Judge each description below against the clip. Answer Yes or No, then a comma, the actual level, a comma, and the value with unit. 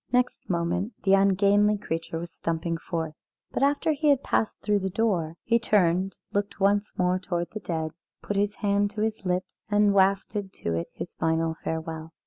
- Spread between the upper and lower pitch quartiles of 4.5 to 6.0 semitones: No, average, 3.6 semitones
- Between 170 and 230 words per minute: Yes, average, 180 wpm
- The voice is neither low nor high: No, high, 195 Hz